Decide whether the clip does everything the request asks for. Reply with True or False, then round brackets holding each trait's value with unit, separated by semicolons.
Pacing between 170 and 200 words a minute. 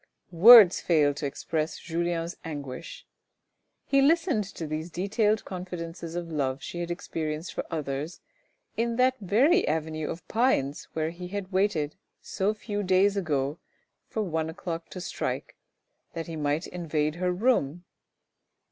False (145 wpm)